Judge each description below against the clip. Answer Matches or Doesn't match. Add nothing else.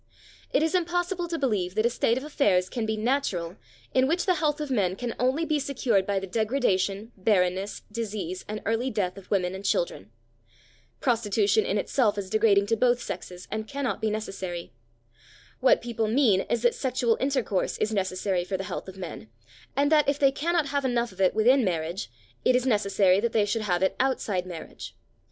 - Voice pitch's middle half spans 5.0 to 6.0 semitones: Matches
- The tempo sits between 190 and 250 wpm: Matches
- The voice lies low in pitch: Doesn't match